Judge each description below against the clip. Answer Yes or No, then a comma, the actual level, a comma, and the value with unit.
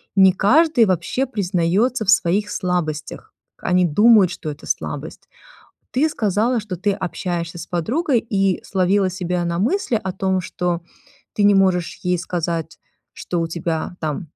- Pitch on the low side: No, medium, 185 Hz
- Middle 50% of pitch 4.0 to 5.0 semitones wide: No, average, 3.3 semitones